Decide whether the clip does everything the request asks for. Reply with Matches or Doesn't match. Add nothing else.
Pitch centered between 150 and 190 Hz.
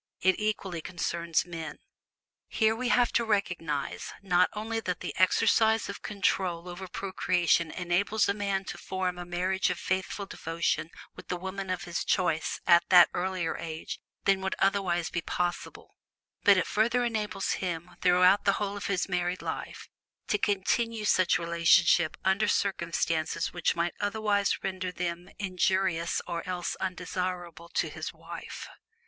Matches